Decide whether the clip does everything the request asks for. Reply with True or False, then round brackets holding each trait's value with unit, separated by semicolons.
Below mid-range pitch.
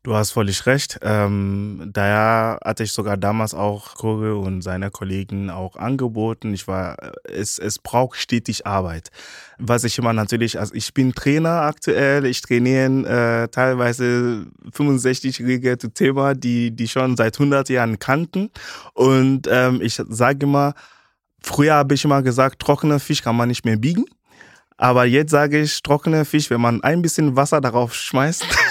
True (120 Hz)